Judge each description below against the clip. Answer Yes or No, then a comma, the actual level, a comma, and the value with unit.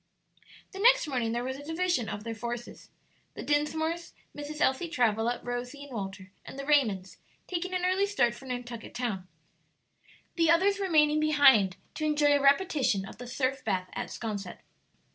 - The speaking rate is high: No, average, 165 wpm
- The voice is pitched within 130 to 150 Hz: No, very high, 270 Hz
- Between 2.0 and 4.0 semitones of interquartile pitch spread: No, average, 5.3 semitones